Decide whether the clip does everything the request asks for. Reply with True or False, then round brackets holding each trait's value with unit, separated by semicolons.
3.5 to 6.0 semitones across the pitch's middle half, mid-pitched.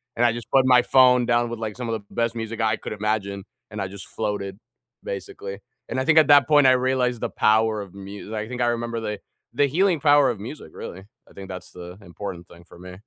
False (4.1 semitones; 110 Hz)